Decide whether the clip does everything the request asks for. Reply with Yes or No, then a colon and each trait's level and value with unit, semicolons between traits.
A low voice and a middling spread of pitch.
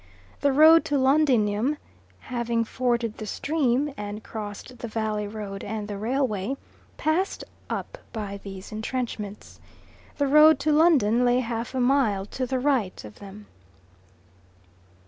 No: high, 235 Hz; average, 4.7 semitones